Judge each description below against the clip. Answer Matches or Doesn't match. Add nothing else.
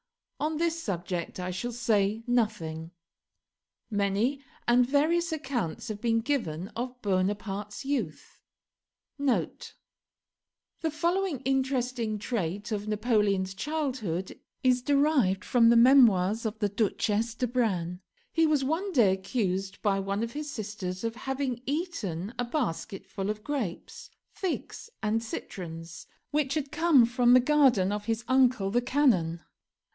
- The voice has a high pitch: Matches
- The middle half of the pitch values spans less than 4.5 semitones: Doesn't match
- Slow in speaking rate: Matches